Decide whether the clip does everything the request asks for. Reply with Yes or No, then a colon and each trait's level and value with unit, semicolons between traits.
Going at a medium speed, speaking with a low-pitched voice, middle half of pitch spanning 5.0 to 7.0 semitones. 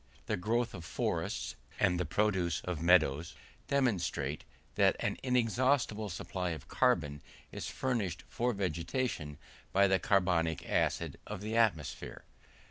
No: slow, 130 wpm; very low, 95 Hz; average, 5.3 semitones